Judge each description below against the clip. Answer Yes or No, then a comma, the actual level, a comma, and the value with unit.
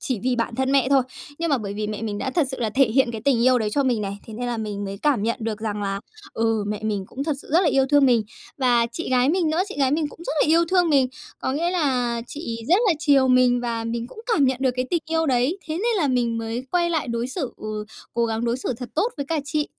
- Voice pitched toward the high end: Yes, very high, 255 Hz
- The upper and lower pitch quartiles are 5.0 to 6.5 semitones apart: No, average, 4.3 semitones